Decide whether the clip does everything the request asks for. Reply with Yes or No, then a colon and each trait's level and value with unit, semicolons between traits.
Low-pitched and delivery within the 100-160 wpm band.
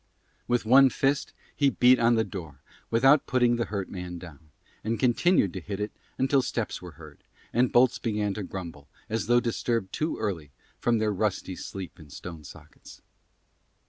No: low, 110 Hz; average, 175 wpm